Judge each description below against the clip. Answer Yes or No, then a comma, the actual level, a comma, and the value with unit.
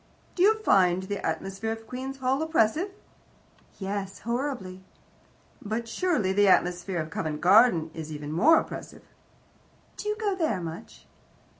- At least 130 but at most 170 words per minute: Yes, average, 140 wpm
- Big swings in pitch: Yes, wide, 6.8 semitones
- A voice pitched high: Yes, high, 205 Hz